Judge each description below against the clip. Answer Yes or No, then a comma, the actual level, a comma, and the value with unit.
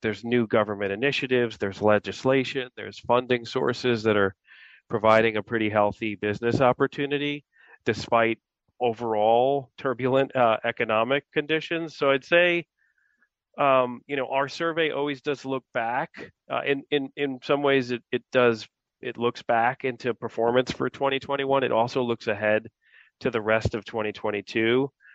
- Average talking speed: Yes, average, 145 wpm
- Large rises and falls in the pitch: No, average, 3.7 semitones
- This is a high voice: No, low, 125 Hz